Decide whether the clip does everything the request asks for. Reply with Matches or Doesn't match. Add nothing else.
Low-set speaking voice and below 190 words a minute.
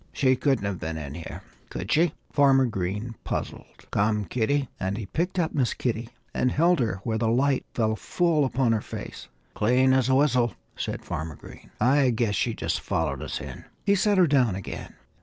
Doesn't match